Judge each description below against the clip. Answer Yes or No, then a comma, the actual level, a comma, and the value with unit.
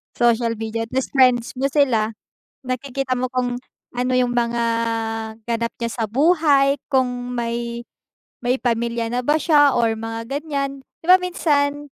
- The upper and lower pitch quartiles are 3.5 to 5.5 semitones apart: No, average, 2.9 semitones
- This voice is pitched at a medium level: No, very high, 250 Hz